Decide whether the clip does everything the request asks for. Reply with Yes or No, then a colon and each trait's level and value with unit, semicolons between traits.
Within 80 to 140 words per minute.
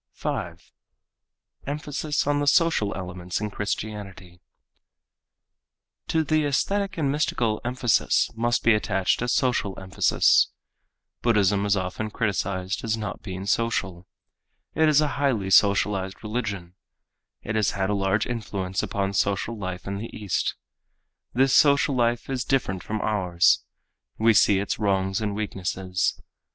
Yes: slow, 135 wpm